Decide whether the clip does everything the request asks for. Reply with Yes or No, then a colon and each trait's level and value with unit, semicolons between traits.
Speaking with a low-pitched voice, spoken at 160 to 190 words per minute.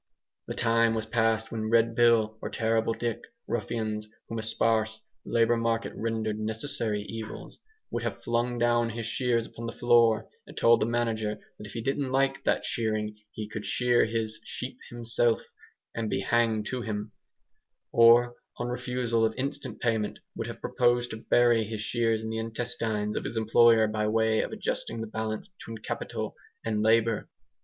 Yes: low, 115 Hz; average, 170 wpm